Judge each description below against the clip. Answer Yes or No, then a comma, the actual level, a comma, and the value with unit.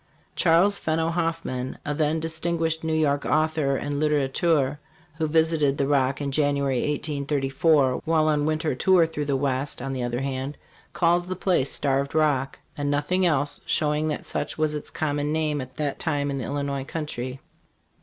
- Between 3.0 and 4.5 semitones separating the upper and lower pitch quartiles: No, narrow, 2.5 semitones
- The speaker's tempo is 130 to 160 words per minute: No, average, 175 wpm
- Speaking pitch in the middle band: Yes, medium, 150 Hz